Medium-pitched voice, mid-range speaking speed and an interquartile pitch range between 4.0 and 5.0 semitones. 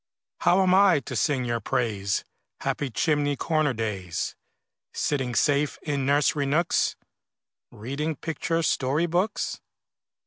No: medium, 145 Hz; slow, 115 wpm; average, 4.4 semitones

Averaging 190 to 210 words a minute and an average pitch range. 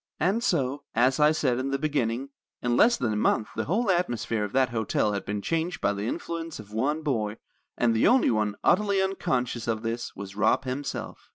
No: fast, 205 wpm; wide, 6.2 semitones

